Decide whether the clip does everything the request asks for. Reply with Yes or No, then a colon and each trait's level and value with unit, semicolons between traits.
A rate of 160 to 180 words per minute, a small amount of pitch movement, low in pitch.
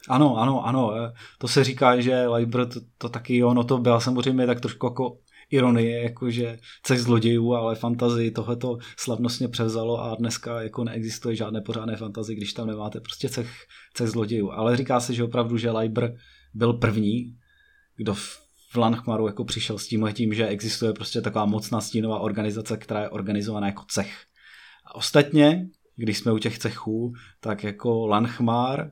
Yes: fast, 170 wpm; narrow, 1.7 semitones; low, 115 Hz